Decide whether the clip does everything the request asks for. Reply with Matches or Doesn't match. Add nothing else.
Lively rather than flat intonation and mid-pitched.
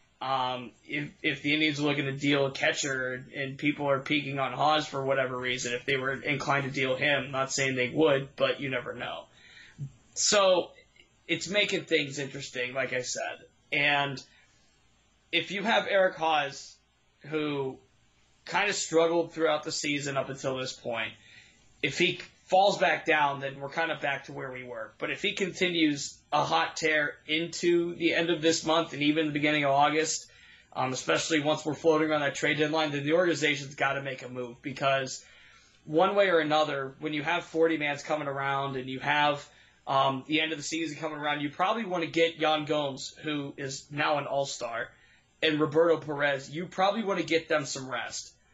Doesn't match